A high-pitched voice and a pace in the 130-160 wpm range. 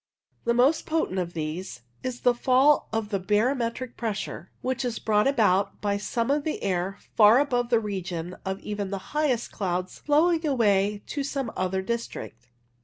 No: high, 220 Hz; average, 170 wpm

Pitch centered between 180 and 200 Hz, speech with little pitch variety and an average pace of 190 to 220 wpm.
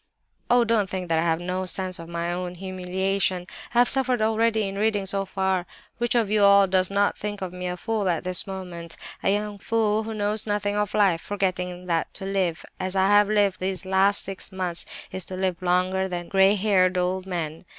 Yes: high, 190 Hz; narrow, 2.2 semitones; average, 200 wpm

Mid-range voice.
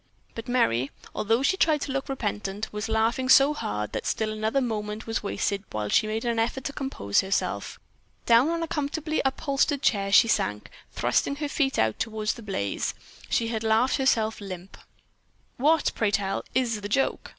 No: high, 225 Hz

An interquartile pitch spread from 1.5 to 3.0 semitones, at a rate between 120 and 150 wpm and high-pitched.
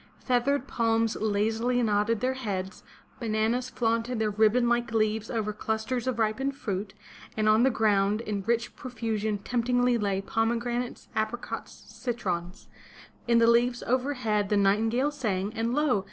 Yes: narrow, 2.5 semitones; average, 140 wpm; high, 225 Hz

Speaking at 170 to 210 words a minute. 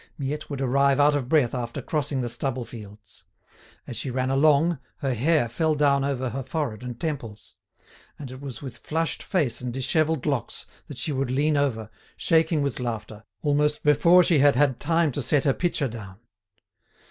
Yes: average, 180 wpm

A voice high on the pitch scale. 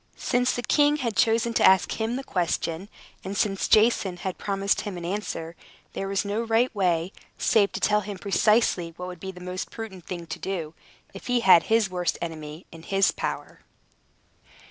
Yes: high, 195 Hz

